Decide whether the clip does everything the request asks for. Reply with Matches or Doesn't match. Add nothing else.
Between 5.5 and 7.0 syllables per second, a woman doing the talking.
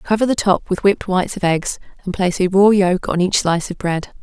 Matches